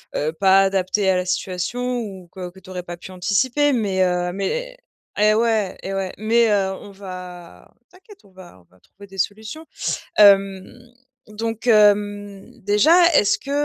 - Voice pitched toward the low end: No, high, 200 Hz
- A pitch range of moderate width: Yes, average, 3.2 semitones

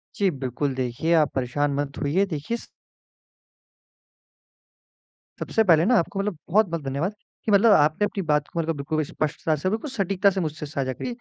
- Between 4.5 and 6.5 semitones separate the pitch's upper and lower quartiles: Yes, wide, 5.5 semitones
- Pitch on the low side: No, medium, 160 Hz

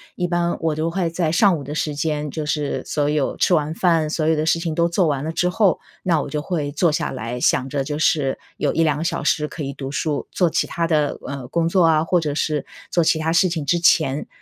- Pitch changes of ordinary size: No, narrow, 2.3 semitones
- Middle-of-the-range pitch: Yes, medium, 155 Hz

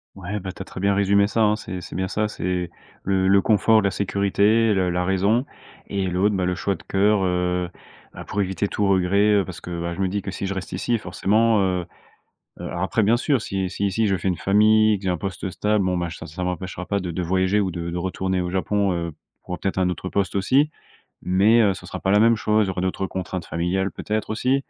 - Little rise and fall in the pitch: Yes, narrow, 2.2 semitones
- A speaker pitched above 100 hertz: No, very low, 95 Hz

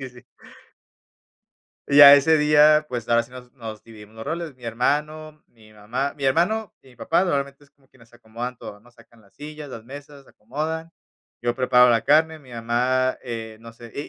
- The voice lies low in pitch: Yes, low, 130 Hz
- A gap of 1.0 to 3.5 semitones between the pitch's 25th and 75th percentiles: No, average, 4.1 semitones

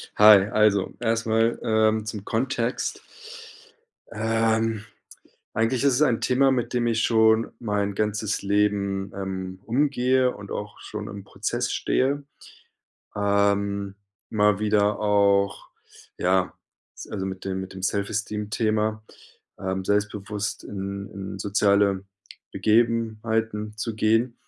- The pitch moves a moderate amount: No, narrow, 2.0 semitones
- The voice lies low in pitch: Yes, low, 105 Hz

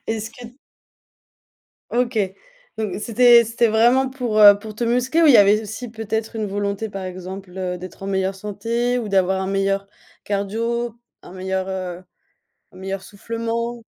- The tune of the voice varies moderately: Yes, average, 3.4 semitones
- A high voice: Yes, high, 215 Hz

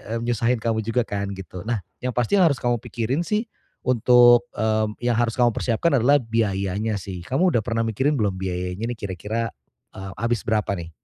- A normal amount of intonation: Yes, average, 3.1 semitones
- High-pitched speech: No, low, 115 Hz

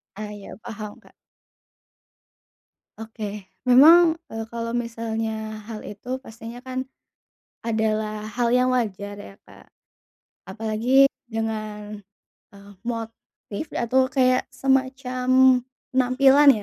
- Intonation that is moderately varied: Yes, average, 3.0 semitones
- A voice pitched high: Yes, high, 230 Hz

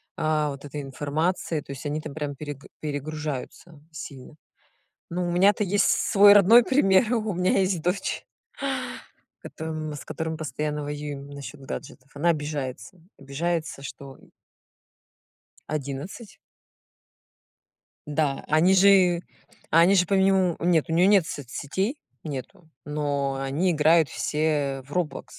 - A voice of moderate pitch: Yes, medium, 155 Hz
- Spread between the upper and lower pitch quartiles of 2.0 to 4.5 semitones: Yes, average, 3.9 semitones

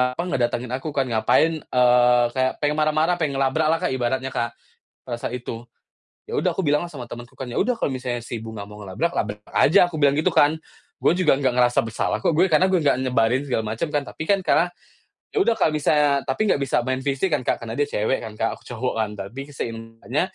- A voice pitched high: No, low, 130 Hz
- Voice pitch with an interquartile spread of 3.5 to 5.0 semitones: Yes, average, 4.4 semitones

